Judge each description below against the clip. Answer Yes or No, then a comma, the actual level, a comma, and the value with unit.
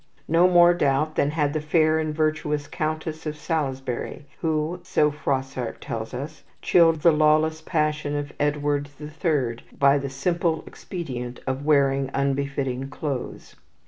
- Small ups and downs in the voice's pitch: Yes, narrow, 2.3 semitones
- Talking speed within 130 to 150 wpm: Yes, average, 145 wpm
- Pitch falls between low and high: Yes, medium, 150 Hz